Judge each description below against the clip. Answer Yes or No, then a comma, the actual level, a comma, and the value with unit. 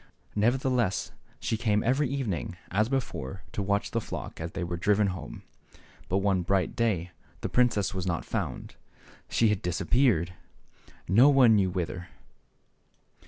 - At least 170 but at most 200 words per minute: No, average, 155 wpm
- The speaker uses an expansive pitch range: No, average, 4.4 semitones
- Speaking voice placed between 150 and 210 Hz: No, low, 100 Hz